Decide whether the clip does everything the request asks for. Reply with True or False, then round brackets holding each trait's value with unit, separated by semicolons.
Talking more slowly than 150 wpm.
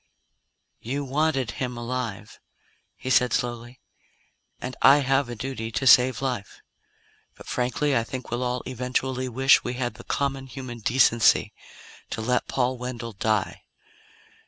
True (140 wpm)